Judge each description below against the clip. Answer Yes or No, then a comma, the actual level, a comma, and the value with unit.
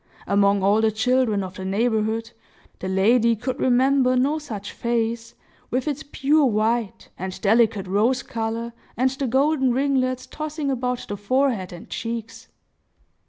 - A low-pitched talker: No, high, 235 Hz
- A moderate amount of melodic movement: Yes, average, 3.4 semitones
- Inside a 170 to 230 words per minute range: No, average, 145 wpm